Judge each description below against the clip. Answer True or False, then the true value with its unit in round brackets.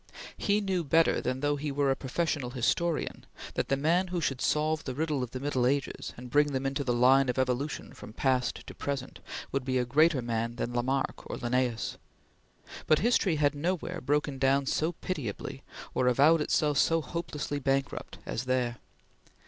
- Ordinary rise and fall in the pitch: True (3.3 semitones)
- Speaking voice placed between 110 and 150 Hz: True (140 Hz)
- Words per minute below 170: False (180 wpm)